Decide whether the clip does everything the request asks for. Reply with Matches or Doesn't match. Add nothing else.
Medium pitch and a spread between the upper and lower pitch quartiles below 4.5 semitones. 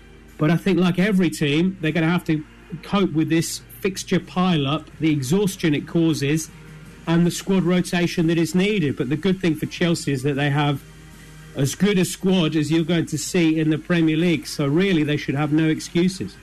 Matches